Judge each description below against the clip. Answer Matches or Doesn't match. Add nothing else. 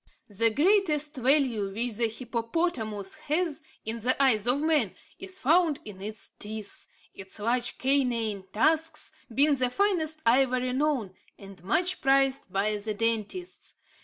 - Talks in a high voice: Matches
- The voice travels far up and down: Matches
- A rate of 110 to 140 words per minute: Matches